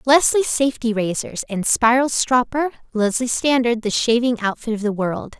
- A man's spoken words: No, female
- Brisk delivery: No, average, 155 wpm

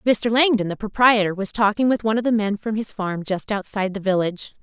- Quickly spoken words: Yes, fast, 235 wpm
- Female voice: Yes, female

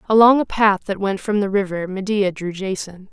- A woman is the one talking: Yes, female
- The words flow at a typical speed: No, fast, 210 wpm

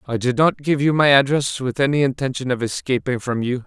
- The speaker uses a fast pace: Yes, fast, 230 wpm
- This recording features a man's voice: Yes, male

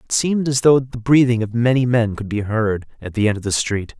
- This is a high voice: No, low, 120 Hz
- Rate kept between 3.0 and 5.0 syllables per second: No, 5.7 syllables/s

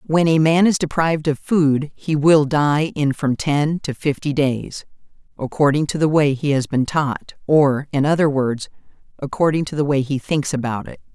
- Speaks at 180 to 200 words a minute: Yes, average, 195 wpm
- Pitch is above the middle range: No, medium, 145 Hz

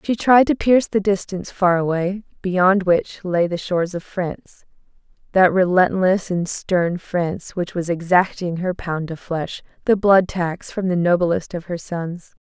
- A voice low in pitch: No, medium, 180 Hz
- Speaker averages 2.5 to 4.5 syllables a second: Yes, 4.3 syllables/s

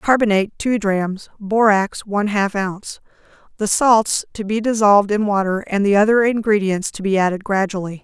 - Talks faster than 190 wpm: No, average, 165 wpm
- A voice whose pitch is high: Yes, high, 205 Hz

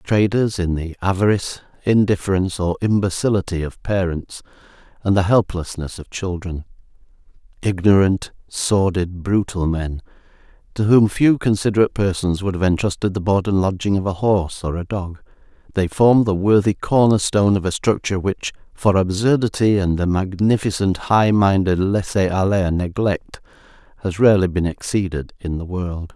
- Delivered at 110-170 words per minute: Yes, average, 140 wpm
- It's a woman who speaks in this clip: No, male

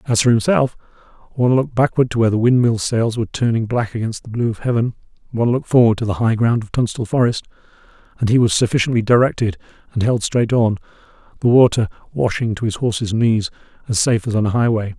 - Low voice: Yes, low, 115 Hz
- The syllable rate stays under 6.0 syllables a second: No, 6.4 syllables/s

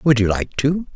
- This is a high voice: No, low, 125 Hz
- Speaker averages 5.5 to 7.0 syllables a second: No, 4.7 syllables/s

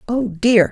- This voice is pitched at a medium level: No, high, 215 Hz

